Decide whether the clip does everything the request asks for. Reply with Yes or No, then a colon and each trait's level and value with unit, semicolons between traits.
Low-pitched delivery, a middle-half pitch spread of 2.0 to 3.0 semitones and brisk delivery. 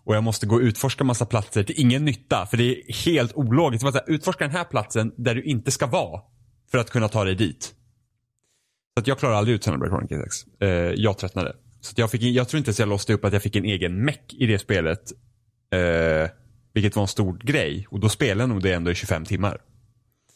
No: low, 115 Hz; average, 3.5 semitones; fast, 225 wpm